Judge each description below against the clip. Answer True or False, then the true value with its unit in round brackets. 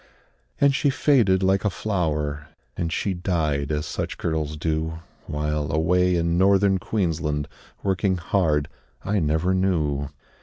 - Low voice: True (85 Hz)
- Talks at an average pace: False (130 wpm)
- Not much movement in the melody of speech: False (4.0 semitones)